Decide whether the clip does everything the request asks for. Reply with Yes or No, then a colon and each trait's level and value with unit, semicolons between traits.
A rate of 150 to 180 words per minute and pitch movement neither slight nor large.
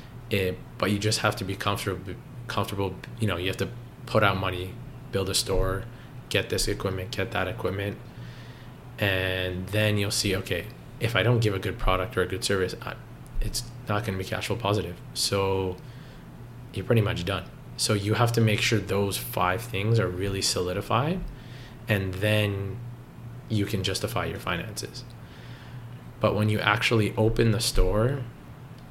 Yes: average, 170 wpm; average, 3.8 semitones